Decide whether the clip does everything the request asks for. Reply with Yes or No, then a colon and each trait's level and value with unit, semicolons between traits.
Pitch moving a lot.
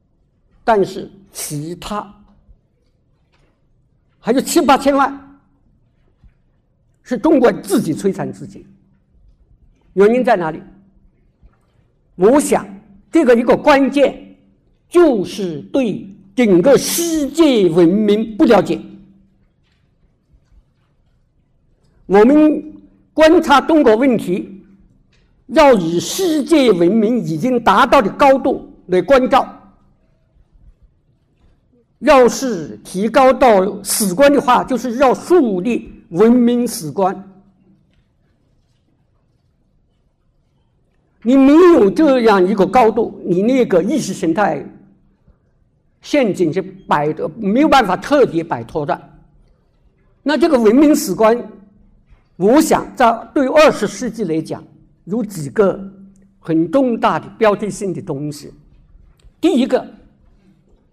Yes: wide, 6.6 semitones